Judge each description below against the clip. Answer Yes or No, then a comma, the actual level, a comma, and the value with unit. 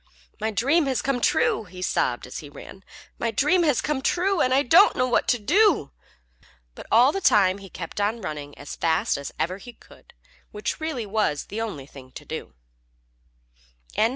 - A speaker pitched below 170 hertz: No, high, 220 Hz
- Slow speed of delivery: No, average, 185 wpm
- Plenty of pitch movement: Yes, wide, 7.1 semitones